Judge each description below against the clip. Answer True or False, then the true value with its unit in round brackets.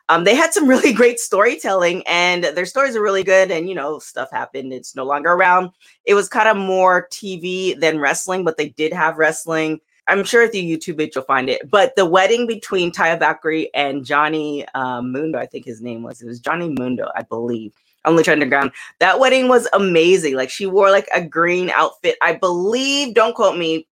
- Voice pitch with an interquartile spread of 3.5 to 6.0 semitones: True (4.2 semitones)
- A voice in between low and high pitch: True (175 Hz)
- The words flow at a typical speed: False (210 wpm)